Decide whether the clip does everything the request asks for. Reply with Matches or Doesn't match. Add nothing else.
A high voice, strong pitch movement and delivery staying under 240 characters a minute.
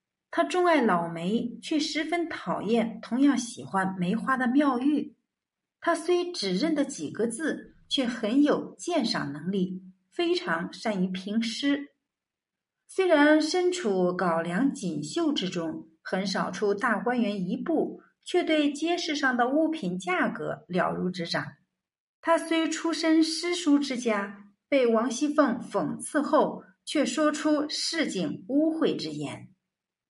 Matches